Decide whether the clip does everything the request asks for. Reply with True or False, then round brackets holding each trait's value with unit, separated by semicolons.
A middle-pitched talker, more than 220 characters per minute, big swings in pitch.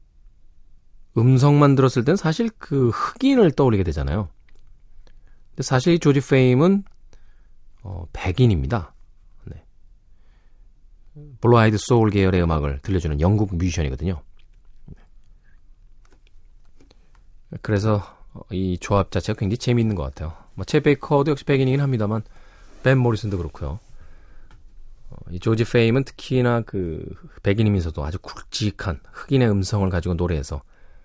False (105 Hz; 280 characters per minute; 7.2 semitones)